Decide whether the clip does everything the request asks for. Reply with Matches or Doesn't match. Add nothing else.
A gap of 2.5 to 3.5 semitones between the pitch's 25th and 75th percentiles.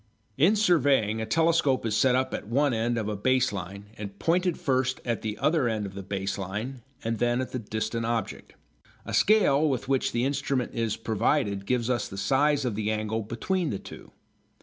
Doesn't match